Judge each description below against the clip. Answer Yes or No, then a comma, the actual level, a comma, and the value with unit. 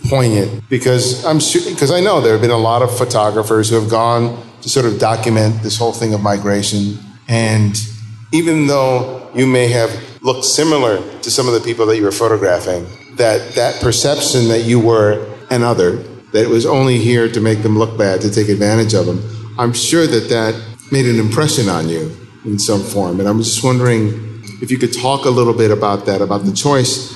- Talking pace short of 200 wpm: No, fast, 205 wpm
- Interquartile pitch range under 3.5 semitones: Yes, average, 2.8 semitones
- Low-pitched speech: Yes, low, 115 Hz